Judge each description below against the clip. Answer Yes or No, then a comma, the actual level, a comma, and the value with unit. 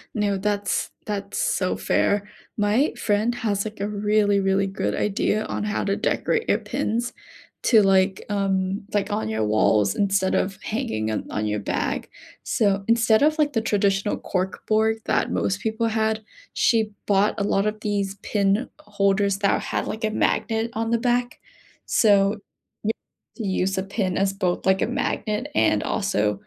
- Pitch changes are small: Yes, narrow, 2.1 semitones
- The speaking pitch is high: Yes, high, 205 Hz